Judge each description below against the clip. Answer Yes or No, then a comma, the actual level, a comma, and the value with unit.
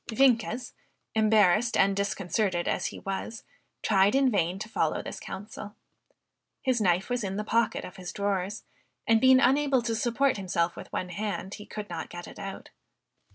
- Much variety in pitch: No, average, 3.3 semitones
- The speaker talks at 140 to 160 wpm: No, average, 170 wpm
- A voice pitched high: Yes, high, 210 Hz